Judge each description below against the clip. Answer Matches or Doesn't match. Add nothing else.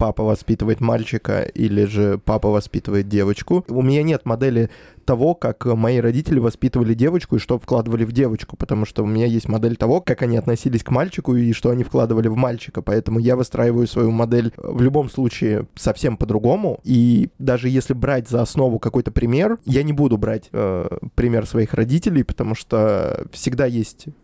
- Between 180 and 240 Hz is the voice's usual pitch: Doesn't match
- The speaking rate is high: Matches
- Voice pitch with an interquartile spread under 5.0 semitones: Matches